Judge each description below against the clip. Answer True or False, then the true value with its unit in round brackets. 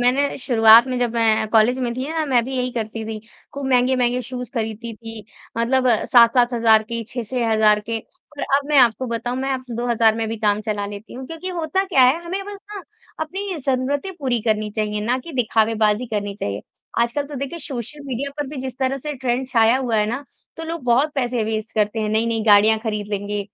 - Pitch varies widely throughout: False (3.2 semitones)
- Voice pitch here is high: True (240 Hz)